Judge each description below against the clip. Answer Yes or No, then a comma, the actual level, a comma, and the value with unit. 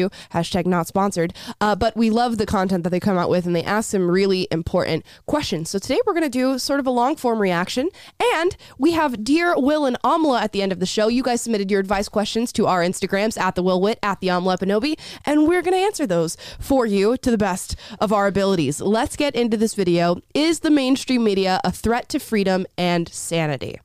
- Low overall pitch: No, high, 210 Hz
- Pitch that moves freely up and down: Yes, wide, 5.7 semitones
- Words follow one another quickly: Yes, fast, 230 wpm